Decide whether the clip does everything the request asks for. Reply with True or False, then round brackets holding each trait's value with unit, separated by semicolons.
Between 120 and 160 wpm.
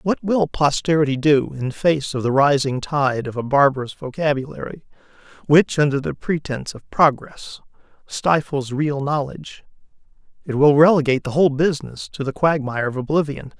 True (150 wpm)